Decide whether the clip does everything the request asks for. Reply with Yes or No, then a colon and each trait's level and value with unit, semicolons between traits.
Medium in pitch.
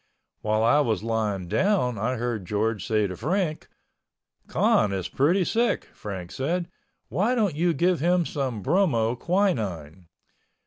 No: low, 125 Hz